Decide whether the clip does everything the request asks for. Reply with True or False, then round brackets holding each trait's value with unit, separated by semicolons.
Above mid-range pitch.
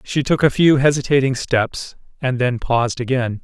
False (130 Hz)